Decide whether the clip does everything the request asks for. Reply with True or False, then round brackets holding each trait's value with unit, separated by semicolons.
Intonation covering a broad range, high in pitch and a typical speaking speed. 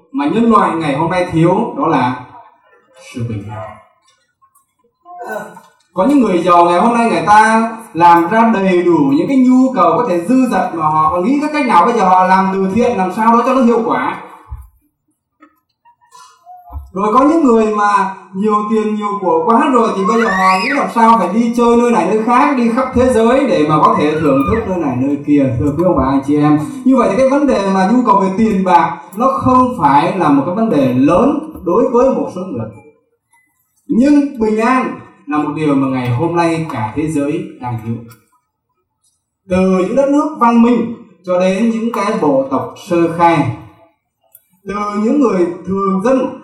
True (6.8 semitones; 215 Hz; 205 wpm)